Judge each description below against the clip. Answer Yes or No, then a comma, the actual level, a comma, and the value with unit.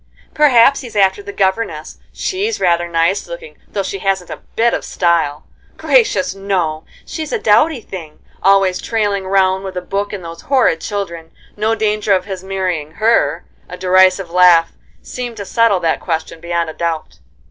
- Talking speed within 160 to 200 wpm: Yes, average, 170 wpm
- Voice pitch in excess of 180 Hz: Yes, high, 190 Hz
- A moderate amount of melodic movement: Yes, average, 3.8 semitones